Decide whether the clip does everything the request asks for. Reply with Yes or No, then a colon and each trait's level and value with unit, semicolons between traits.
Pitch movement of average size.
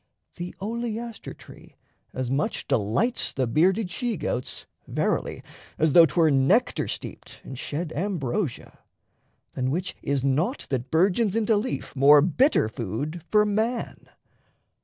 No: wide, 7.7 semitones